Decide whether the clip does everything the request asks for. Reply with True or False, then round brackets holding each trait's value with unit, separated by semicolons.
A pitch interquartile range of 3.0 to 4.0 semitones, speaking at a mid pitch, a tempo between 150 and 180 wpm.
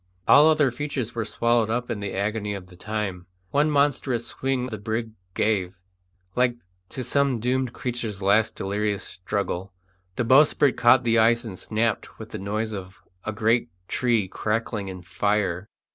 False (3.3 semitones; 110 Hz; 160 wpm)